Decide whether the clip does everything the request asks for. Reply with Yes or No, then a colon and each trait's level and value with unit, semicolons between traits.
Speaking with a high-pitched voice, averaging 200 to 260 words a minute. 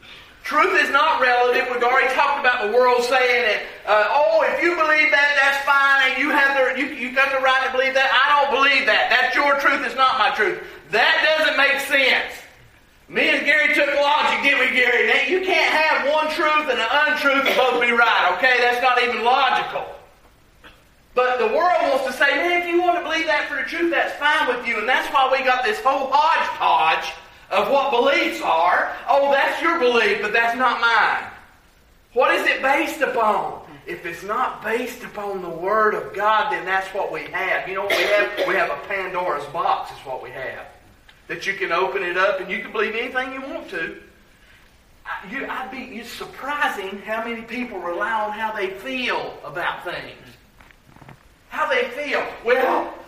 Yes: very high, 260 Hz; fast, 205 wpm